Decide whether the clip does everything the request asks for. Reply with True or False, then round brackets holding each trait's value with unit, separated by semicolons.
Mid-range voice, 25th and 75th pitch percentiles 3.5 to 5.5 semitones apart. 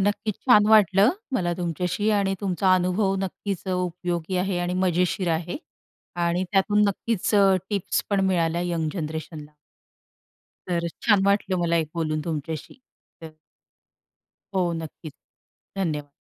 False (180 Hz; 2.8 semitones)